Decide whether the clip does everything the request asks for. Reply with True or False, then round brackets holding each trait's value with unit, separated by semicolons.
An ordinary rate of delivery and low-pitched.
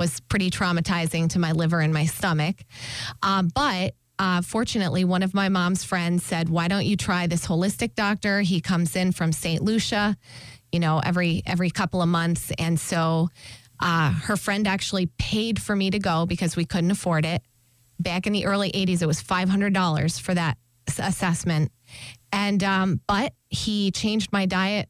False (180 wpm; 175 Hz)